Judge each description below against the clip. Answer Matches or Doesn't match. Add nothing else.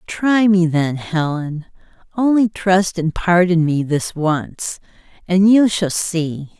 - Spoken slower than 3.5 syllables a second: Matches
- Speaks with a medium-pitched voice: Matches